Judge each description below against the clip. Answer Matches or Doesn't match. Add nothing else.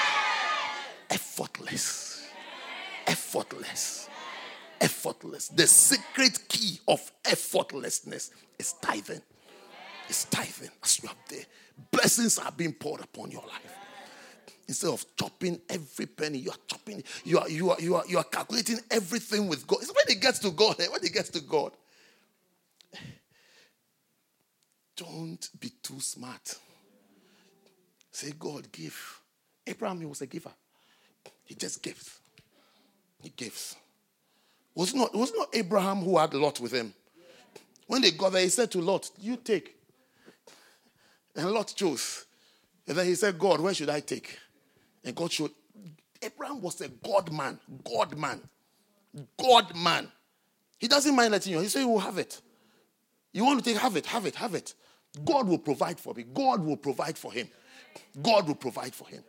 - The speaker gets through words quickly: Doesn't match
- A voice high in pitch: Matches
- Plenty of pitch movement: Matches